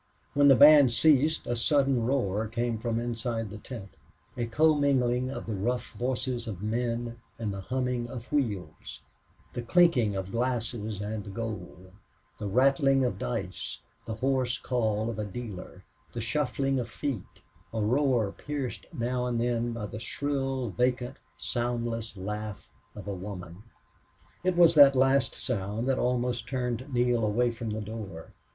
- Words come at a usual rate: Yes, average, 155 wpm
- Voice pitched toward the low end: Yes, low, 120 Hz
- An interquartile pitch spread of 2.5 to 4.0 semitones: Yes, average, 3.3 semitones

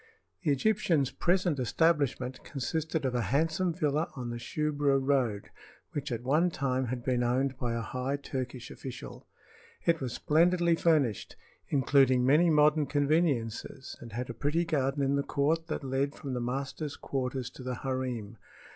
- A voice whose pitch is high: No, low, 135 Hz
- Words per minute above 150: Yes, average, 160 wpm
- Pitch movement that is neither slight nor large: Yes, average, 3.2 semitones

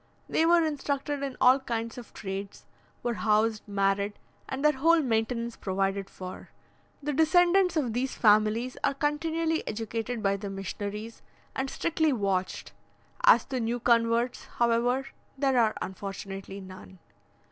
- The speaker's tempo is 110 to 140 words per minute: Yes, slow, 135 wpm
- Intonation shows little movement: No, average, 5.3 semitones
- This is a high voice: Yes, high, 235 Hz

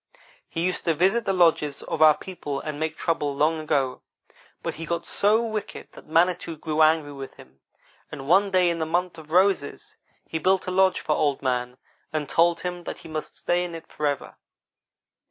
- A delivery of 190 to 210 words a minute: Yes, average, 195 wpm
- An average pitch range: Yes, average, 3.1 semitones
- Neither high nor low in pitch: Yes, medium, 160 Hz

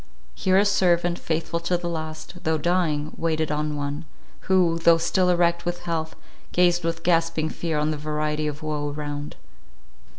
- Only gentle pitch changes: Yes, narrow, 2.3 semitones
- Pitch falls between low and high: Yes, medium, 165 Hz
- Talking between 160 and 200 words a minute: Yes, average, 165 wpm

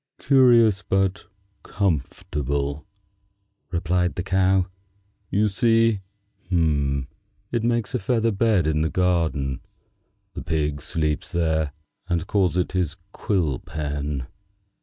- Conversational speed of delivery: No, slow, 105 wpm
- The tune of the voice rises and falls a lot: No, average, 4.8 semitones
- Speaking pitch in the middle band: No, very low, 90 Hz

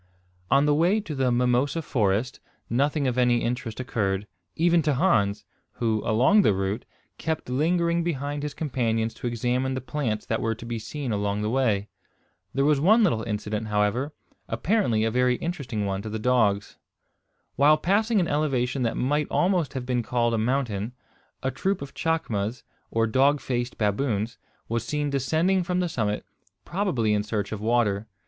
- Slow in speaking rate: No, average, 170 wpm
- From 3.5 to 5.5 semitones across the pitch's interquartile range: Yes, average, 5.1 semitones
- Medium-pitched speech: No, low, 125 Hz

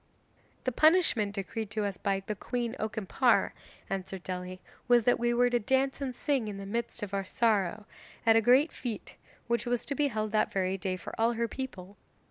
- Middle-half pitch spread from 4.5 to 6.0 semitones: No, average, 3.7 semitones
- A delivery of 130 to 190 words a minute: No, average, 200 wpm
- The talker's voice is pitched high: Yes, high, 225 Hz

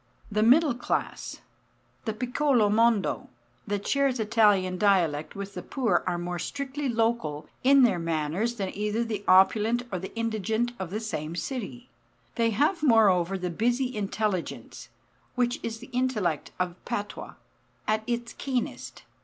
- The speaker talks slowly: No, average, 145 wpm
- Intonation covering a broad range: No, average, 4.3 semitones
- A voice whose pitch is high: Yes, high, 220 Hz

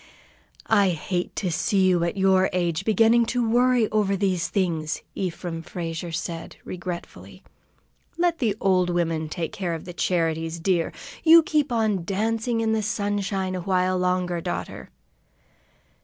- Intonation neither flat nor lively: Yes, average, 4.0 semitones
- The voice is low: No, medium, 185 Hz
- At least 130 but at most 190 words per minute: Yes, average, 145 wpm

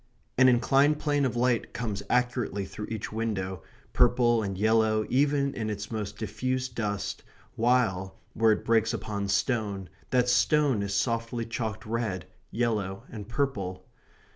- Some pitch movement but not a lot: Yes, average, 3.4 semitones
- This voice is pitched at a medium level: No, low, 115 Hz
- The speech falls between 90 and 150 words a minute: Yes, average, 140 wpm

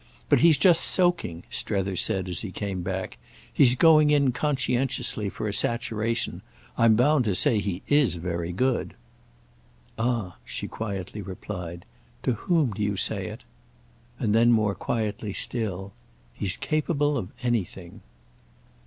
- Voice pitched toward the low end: Yes, low, 110 Hz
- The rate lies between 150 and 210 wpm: No, average, 140 wpm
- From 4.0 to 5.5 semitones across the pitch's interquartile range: Yes, average, 5.2 semitones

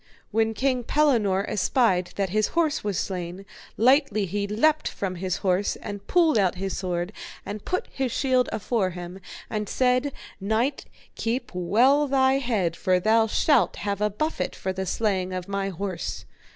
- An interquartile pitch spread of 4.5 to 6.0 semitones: Yes, average, 5.1 semitones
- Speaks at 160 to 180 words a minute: Yes, average, 165 wpm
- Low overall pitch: No, high, 210 Hz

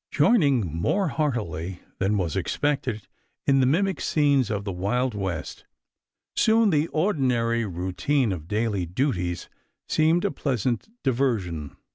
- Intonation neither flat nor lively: No, wide, 7.6 semitones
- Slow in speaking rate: Yes, slow, 125 wpm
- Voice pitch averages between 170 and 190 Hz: No, low, 120 Hz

